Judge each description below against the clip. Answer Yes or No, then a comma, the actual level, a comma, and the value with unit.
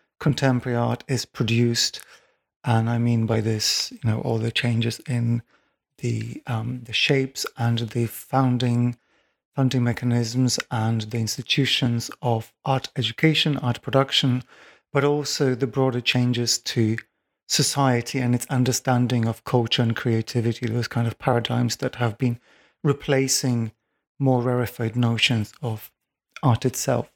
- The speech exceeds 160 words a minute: No, slow, 135 wpm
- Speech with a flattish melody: Yes, narrow, 2.0 semitones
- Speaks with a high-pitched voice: No, low, 120 Hz